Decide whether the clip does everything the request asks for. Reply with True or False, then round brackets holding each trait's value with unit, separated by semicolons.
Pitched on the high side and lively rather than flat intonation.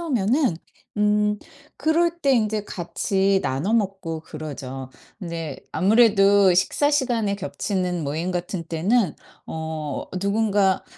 False (195 Hz; 4.7 semitones)